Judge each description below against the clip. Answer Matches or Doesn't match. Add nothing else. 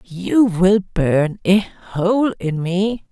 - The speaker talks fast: Doesn't match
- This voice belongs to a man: Doesn't match